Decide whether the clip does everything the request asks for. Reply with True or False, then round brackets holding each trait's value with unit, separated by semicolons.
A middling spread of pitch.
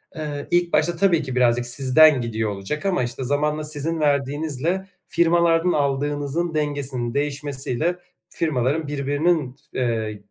True (3.8 semitones)